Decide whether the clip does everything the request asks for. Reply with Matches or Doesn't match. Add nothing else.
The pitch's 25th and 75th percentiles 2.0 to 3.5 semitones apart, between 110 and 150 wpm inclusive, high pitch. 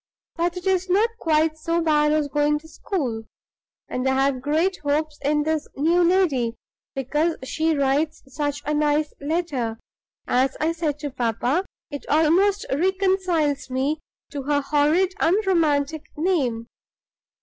Matches